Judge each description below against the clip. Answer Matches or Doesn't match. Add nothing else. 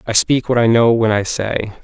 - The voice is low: Matches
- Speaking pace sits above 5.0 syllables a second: Doesn't match